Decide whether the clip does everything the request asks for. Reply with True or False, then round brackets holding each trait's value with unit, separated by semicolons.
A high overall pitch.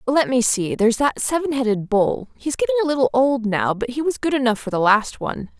True (250 Hz)